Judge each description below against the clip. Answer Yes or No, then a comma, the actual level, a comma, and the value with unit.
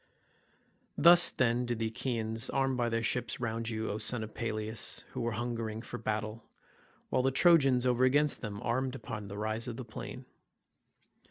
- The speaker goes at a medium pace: Yes, average, 175 wpm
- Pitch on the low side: Yes, low, 115 Hz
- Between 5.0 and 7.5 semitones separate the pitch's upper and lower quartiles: No, average, 2.7 semitones